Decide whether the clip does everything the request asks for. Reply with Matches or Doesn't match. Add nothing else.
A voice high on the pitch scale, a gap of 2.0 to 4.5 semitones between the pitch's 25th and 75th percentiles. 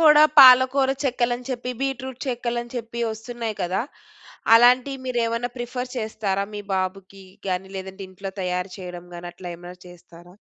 Doesn't match